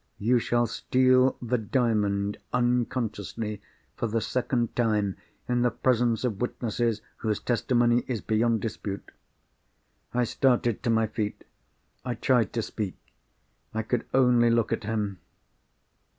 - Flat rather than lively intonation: Yes, narrow, 2.2 semitones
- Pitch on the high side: No, low, 115 Hz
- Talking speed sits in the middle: No, slow, 130 wpm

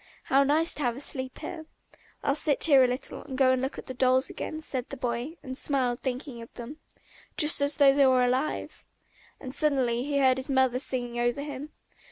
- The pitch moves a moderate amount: No, narrow, 2.2 semitones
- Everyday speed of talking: No, fast, 215 wpm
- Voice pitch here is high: Yes, very high, 265 Hz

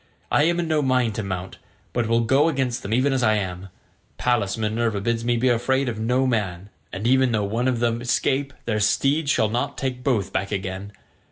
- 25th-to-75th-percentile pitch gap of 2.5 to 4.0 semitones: Yes, average, 3.7 semitones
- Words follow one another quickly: Yes, fast, 210 wpm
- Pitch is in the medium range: No, low, 120 Hz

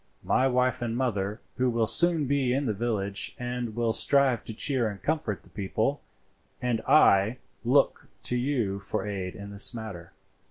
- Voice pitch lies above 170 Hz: No, low, 120 Hz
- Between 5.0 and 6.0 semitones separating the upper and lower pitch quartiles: No, average, 3.9 semitones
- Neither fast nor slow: Yes, average, 170 wpm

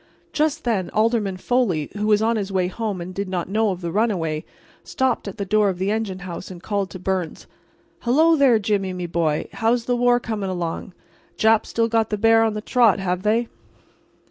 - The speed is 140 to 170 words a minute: No, average, 200 wpm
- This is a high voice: Yes, high, 210 Hz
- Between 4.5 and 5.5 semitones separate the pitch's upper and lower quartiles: No, average, 3.5 semitones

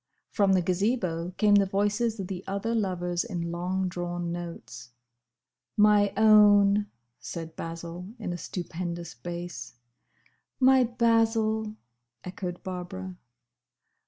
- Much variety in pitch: No, average, 3.2 semitones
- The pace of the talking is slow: Yes, slow, 110 wpm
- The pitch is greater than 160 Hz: Yes, medium, 185 Hz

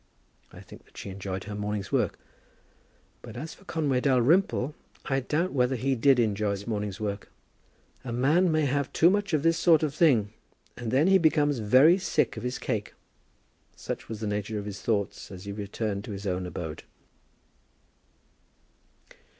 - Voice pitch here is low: Yes, low, 125 Hz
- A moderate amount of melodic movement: No, wide, 6.5 semitones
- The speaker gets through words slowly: No, average, 175 wpm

